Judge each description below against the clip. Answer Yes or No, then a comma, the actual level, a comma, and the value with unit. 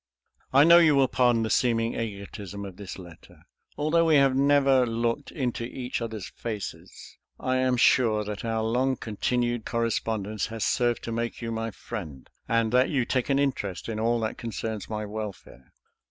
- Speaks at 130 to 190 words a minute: Yes, average, 175 wpm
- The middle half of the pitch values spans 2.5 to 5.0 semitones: Yes, average, 3.0 semitones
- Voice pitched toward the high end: No, low, 115 Hz